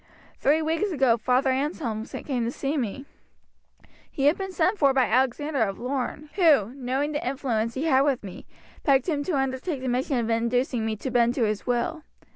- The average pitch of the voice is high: Yes, very high, 265 Hz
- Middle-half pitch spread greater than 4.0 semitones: No, average, 3.5 semitones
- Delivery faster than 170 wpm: Yes, average, 195 wpm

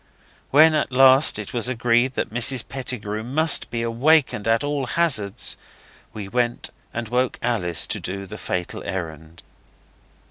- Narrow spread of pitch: No, average, 4.2 semitones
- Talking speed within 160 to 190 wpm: No, average, 145 wpm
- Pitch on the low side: Yes, low, 120 Hz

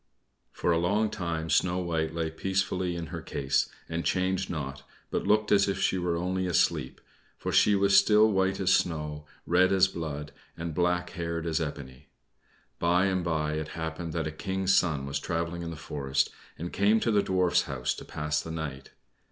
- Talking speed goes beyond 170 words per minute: Yes, average, 190 wpm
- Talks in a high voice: No, very low, 85 Hz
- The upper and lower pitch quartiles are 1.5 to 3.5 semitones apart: Yes, average, 3.0 semitones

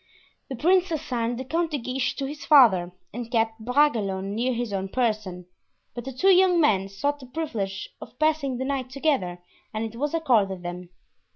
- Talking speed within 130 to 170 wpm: No, average, 185 wpm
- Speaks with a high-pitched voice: Yes, high, 245 Hz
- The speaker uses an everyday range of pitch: No, wide, 6.0 semitones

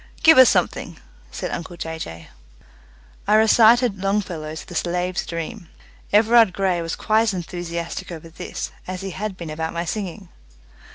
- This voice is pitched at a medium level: Yes, medium, 180 Hz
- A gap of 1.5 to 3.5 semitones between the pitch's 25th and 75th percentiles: No, average, 3.9 semitones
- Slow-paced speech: No, average, 155 wpm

